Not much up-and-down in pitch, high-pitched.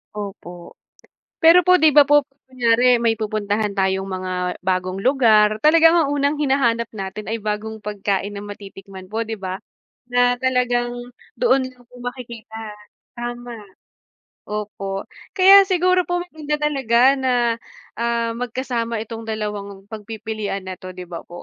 No: average, 4.2 semitones; high, 225 Hz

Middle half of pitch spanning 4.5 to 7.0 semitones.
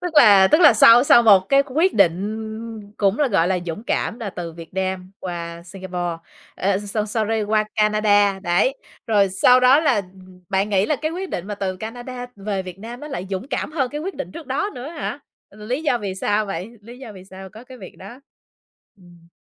Yes: average, 4.8 semitones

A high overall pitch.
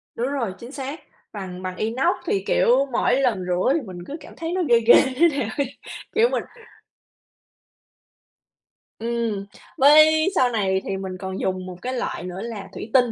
Yes: high, 235 Hz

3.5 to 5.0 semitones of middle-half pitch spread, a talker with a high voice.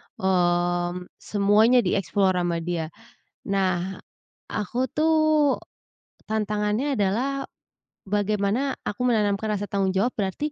Yes: average, 4.3 semitones; high, 205 Hz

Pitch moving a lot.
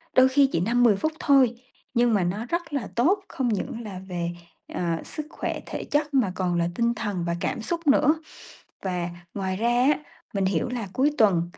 Yes: wide, 5.9 semitones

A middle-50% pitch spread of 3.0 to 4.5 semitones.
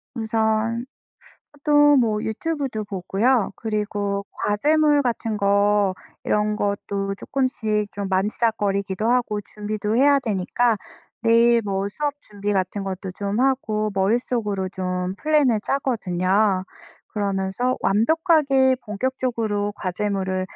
Yes: average, 3.5 semitones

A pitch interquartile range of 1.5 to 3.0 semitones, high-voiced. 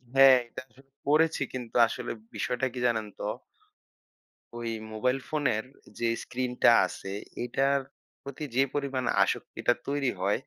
No: average, 2.7 semitones; low, 130 Hz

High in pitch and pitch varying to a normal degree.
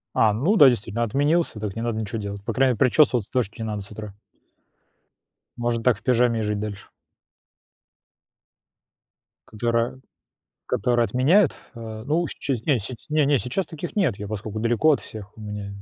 No: low, 115 Hz; average, 3.7 semitones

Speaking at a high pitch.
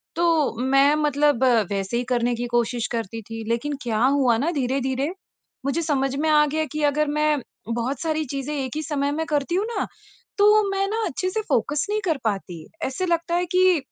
Yes: very high, 285 Hz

